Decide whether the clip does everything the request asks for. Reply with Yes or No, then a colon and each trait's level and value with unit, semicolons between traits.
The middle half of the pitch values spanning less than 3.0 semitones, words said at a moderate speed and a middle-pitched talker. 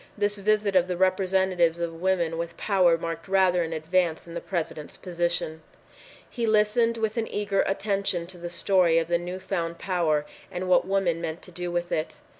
Yes: narrow, 2.4 semitones; average, 190 wpm; medium, 180 Hz